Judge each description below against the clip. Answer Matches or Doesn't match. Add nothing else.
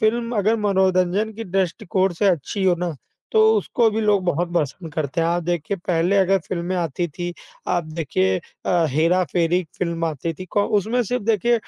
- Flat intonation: Doesn't match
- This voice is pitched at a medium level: Matches